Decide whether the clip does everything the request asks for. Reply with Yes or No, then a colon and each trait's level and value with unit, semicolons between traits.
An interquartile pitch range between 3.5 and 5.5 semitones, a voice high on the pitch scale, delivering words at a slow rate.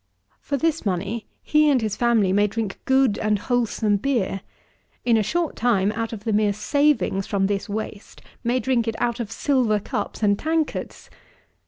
No: average, 3.8 semitones; high, 225 Hz; average, 175 wpm